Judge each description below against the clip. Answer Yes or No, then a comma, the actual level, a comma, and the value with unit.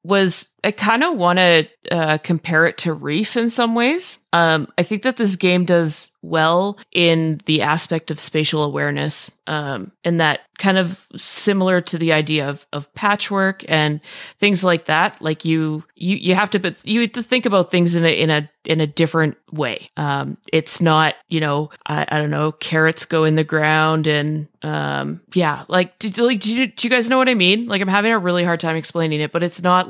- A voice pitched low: No, medium, 170 Hz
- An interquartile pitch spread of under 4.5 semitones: Yes, average, 3.9 semitones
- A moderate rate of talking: No, fast, 215 wpm